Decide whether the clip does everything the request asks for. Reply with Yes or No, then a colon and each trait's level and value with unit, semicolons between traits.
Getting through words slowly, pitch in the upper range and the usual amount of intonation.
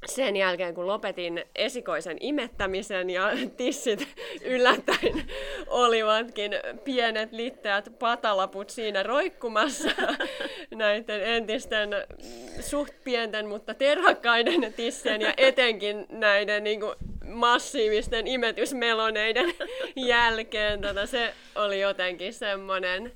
Yes: slow, 90 wpm; high, 230 Hz; average, 4.3 semitones